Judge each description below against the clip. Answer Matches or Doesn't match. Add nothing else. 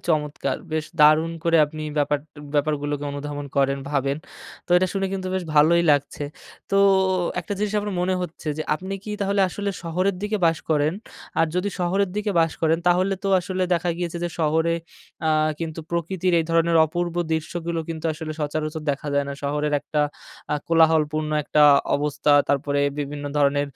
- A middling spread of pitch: Matches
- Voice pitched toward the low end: Doesn't match